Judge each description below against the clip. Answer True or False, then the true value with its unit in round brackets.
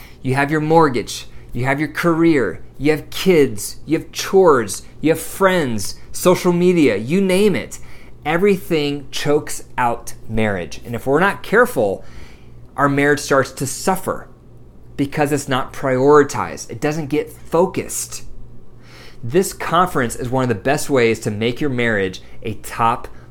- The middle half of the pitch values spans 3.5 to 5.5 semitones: True (5.1 semitones)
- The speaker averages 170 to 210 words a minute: False (150 wpm)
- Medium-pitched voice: True (145 Hz)